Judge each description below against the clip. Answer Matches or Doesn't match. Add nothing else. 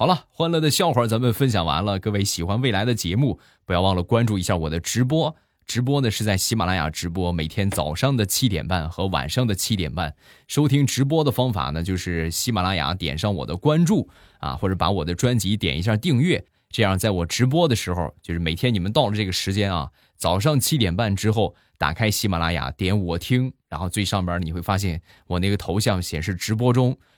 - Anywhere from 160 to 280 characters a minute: Doesn't match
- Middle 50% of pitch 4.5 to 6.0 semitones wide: Matches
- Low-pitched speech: Matches